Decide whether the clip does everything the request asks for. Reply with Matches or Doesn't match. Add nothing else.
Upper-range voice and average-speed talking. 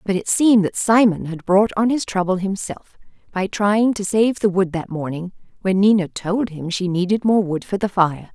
Doesn't match